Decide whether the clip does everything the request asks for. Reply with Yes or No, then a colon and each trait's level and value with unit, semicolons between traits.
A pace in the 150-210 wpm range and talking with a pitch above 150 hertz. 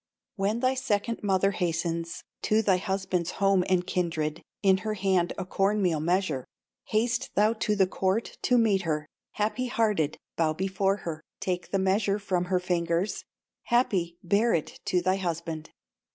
Yes: average, 160 wpm; high, 190 Hz